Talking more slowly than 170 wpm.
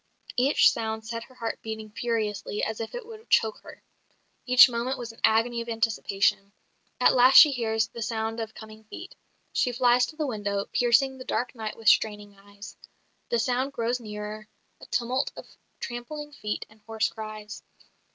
No: average, 175 wpm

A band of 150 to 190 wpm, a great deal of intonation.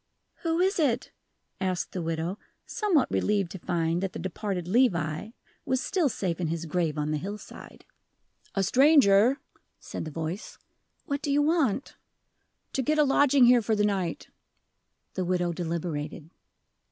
Yes: average, 155 wpm; wide, 7.8 semitones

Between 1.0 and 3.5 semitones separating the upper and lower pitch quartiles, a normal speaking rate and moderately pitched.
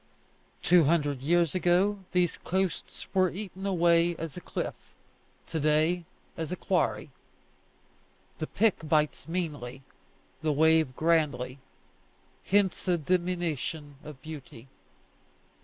No: average, 2.9 semitones; slow, 110 wpm; medium, 165 Hz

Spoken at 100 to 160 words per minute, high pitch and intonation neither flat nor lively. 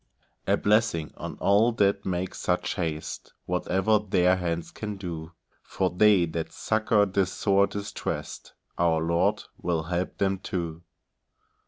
No: slow, 135 wpm; very low, 95 Hz; average, 3.1 semitones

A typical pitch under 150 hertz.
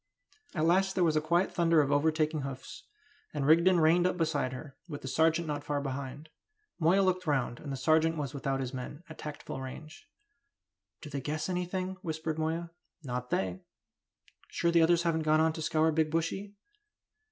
No: medium, 155 Hz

